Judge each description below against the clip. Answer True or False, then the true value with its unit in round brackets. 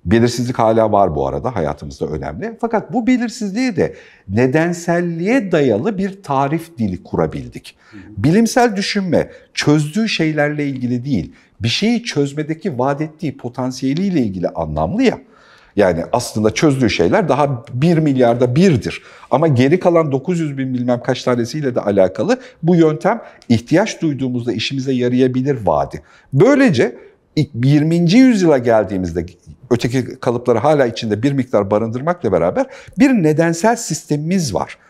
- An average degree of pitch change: False (6.4 semitones)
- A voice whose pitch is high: False (140 Hz)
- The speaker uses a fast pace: False (125 wpm)